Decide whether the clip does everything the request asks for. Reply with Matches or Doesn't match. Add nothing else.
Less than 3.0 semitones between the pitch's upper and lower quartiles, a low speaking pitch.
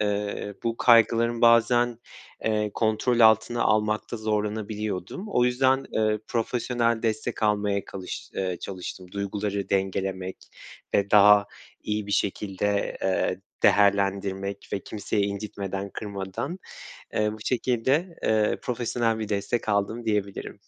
Matches